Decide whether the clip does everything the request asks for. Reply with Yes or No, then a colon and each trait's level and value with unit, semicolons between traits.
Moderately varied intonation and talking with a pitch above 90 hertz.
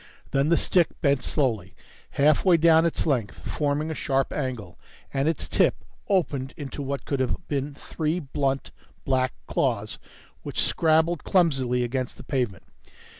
Yes: average, 3.4 semitones; medium, 140 Hz